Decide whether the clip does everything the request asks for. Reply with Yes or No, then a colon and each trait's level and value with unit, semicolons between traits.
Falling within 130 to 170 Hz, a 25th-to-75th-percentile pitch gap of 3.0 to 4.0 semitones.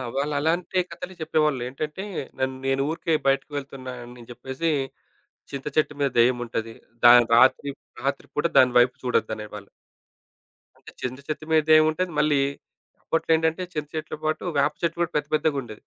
Yes: medium, 140 Hz; average, 3.5 semitones